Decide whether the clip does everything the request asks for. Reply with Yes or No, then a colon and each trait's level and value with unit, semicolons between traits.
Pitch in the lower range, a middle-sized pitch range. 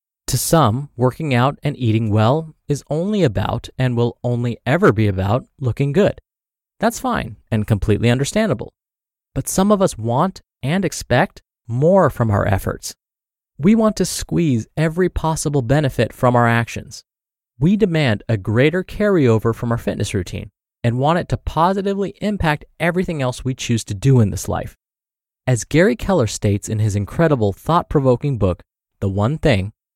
No: low, 125 Hz; wide, 6.4 semitones